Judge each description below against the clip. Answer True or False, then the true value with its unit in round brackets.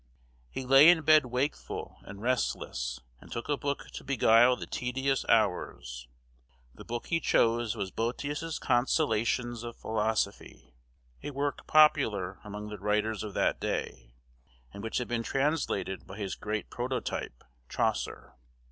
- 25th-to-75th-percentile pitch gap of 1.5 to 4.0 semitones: False (4.5 semitones)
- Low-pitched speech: True (120 Hz)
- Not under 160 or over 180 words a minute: False (140 wpm)